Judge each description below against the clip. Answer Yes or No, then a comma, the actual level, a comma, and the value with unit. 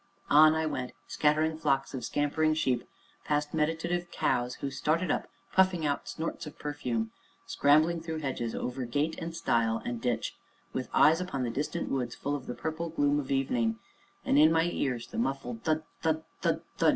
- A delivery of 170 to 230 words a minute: Yes, average, 180 wpm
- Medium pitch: Yes, medium, 145 Hz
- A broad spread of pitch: No, average, 3.9 semitones